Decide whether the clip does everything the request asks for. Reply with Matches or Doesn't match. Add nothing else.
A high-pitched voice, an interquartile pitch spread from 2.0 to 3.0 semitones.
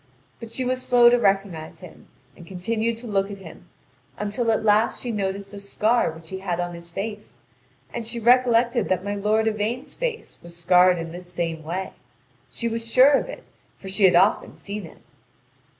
Doesn't match